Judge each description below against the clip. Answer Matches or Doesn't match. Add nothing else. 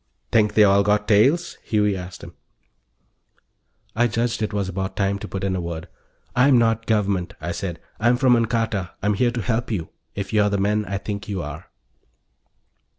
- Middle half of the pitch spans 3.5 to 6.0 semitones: Doesn't match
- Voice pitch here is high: Doesn't match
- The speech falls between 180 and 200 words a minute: Matches